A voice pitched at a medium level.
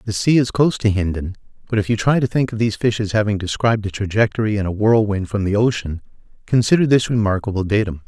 No: low, 105 Hz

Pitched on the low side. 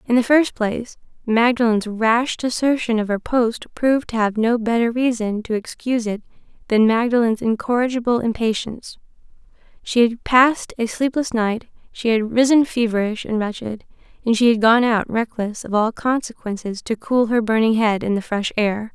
No: high, 230 Hz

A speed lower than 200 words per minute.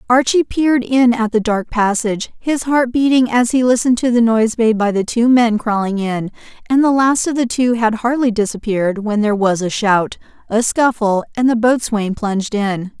No: fast, 205 wpm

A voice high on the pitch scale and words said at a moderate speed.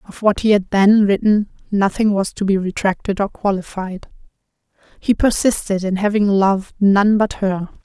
Yes: high, 200 Hz; average, 160 wpm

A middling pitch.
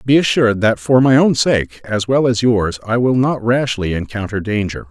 No: low, 115 Hz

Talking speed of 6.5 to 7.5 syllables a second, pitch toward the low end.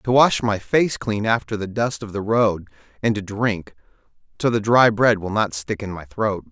No: 4.6 syllables/s; low, 105 Hz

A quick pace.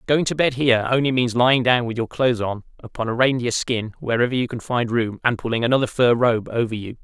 Yes: fast, 240 wpm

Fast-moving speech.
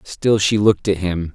Yes: fast, 225 wpm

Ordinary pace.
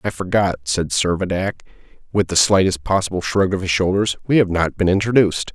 Yes: average, 185 wpm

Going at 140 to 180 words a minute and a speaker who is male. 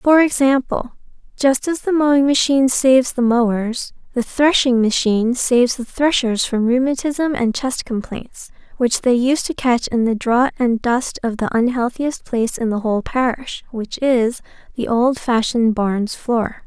No: average, 160 wpm; female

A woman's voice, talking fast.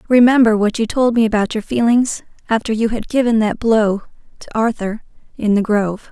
No: female; average, 185 wpm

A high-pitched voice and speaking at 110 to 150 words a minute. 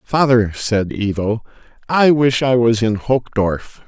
No: low, 115 Hz; average, 140 wpm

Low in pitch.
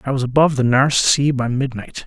Yes: low, 130 Hz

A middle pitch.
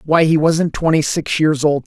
Yes: medium, 155 Hz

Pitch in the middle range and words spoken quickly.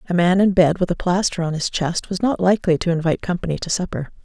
Yes: medium, 175 Hz; fast, 255 wpm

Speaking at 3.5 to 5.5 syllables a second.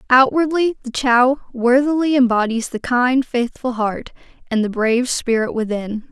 Yes: 4.5 syllables/s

